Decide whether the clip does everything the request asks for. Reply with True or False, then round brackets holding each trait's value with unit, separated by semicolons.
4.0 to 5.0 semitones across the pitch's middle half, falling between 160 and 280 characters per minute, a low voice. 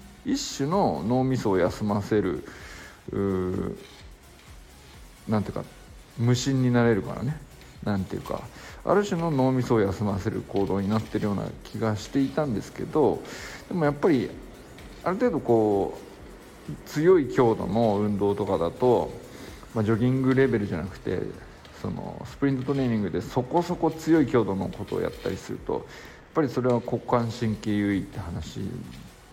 False (4.6 semitones; 315 characters per minute; 115 Hz)